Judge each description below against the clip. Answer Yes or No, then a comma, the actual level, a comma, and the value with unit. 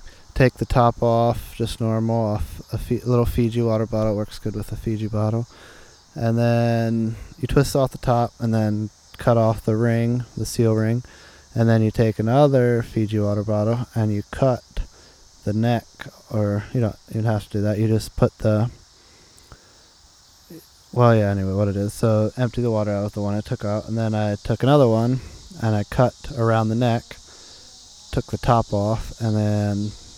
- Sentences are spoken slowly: No, average, 190 wpm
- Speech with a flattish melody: Yes, narrow, 2.2 semitones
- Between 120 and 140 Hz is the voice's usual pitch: No, low, 110 Hz